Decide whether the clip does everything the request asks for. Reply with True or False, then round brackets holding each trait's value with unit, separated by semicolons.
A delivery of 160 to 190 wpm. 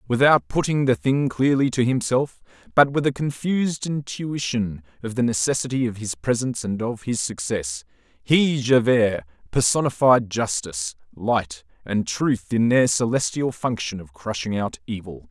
False (145 wpm)